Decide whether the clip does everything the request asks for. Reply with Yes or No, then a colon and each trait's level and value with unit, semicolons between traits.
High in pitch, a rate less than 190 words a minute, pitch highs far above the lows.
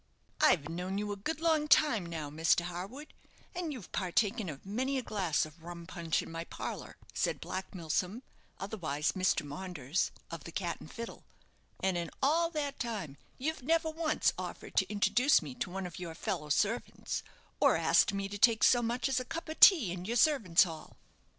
No: high, 195 Hz; average, 195 wpm; wide, 7.0 semitones